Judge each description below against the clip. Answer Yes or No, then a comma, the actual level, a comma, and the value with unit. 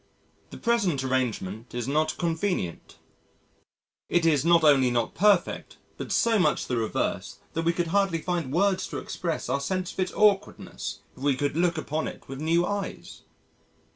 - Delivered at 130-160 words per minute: No, average, 170 wpm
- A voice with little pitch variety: No, wide, 5.4 semitones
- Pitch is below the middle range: No, medium, 165 Hz